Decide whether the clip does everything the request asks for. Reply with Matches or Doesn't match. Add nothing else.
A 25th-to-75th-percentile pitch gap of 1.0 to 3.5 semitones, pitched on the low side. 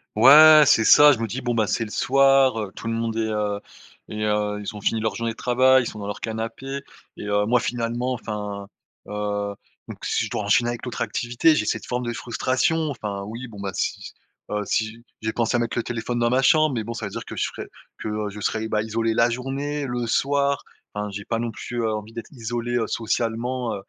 Matches